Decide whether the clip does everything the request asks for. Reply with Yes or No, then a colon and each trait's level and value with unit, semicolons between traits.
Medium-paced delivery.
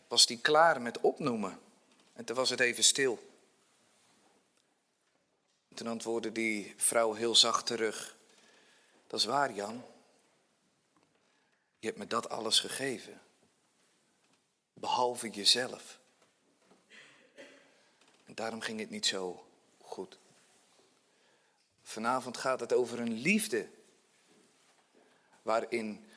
No: slow, 105 wpm